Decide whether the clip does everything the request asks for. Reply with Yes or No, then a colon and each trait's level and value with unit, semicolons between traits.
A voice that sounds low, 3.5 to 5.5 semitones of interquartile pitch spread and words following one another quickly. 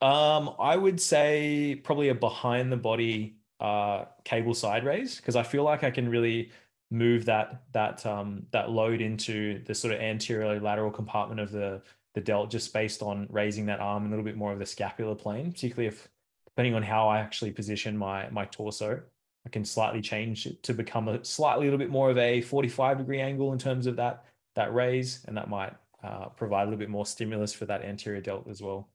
No: low, 110 Hz; average, 3.0 semitones; fast, 215 wpm